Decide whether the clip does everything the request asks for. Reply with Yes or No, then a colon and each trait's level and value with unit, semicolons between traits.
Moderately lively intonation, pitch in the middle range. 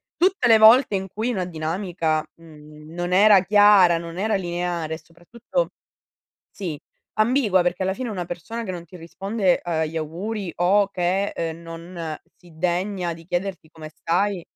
Yes: average, 3.4 semitones; medium, 180 Hz